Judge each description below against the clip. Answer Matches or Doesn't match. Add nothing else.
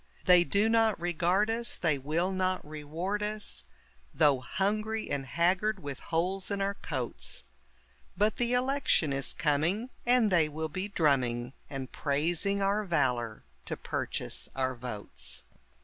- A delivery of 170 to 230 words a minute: Doesn't match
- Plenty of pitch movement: Matches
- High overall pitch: Doesn't match